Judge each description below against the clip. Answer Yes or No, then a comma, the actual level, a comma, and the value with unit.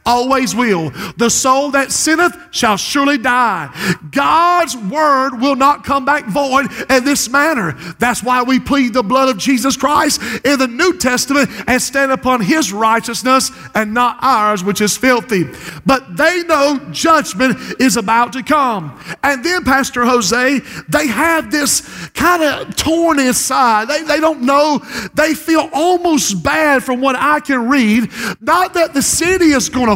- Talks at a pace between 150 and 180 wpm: Yes, average, 165 wpm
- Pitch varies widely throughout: No, average, 3.7 semitones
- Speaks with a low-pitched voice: No, very high, 265 Hz